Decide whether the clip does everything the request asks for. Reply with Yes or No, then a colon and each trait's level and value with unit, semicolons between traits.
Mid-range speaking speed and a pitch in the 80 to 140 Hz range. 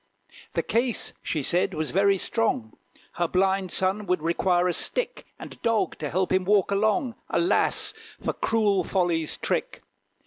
No: average, 150 wpm; high, 190 Hz